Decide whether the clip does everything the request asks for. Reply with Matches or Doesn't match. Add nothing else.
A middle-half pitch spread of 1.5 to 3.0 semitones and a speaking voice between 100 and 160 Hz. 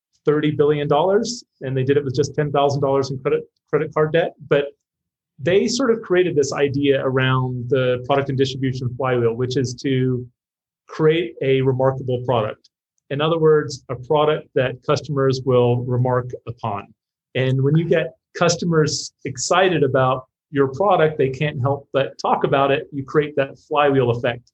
Matches